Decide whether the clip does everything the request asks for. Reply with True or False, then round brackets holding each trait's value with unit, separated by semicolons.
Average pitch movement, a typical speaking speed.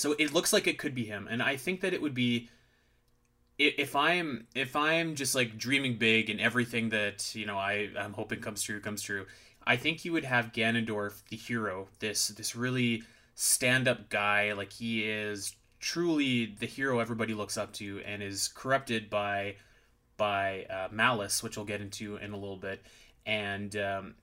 True (3.3 semitones; 190 wpm)